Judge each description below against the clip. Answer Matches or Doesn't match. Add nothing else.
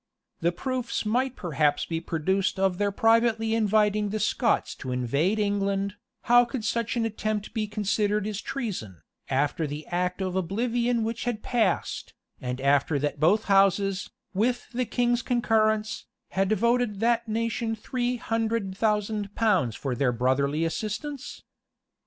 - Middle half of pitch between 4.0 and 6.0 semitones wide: Matches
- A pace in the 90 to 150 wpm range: Matches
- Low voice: Doesn't match